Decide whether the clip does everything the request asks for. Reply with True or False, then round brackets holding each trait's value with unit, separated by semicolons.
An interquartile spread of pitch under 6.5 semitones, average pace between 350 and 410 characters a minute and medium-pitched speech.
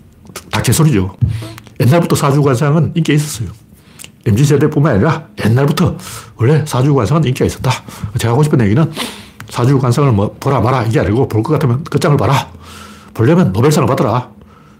False (5.6 semitones; 365 characters per minute; 130 Hz)